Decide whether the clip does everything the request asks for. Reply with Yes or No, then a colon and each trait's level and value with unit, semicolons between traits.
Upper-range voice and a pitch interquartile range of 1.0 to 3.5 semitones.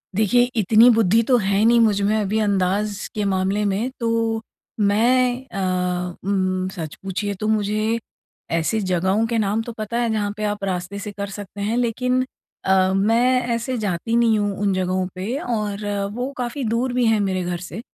Yes: high, 210 Hz; average, 3.1 semitones